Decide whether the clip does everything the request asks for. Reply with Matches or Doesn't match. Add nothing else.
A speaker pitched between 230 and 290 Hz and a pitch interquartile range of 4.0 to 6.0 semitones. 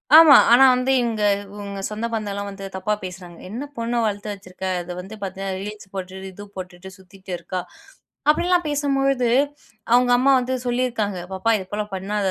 Doesn't match